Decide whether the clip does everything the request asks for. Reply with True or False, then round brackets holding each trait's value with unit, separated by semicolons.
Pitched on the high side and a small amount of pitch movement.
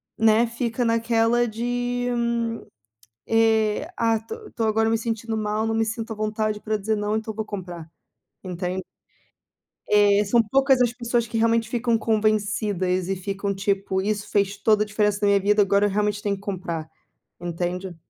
True (215 Hz; 2.1 semitones)